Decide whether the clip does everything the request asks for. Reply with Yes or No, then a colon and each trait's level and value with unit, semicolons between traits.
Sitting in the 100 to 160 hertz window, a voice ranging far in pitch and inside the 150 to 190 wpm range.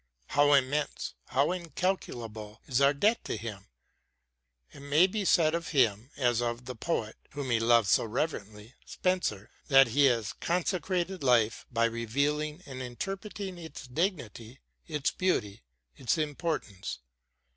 No: low, 135 Hz; wide, 6.3 semitones; average, 140 wpm